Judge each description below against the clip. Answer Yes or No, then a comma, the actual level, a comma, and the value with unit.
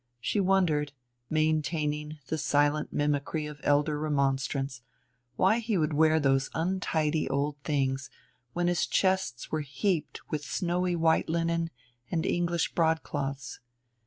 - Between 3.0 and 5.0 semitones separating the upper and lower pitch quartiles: No, narrow, 2.6 semitones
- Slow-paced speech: Yes, slow, 125 wpm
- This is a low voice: No, medium, 155 Hz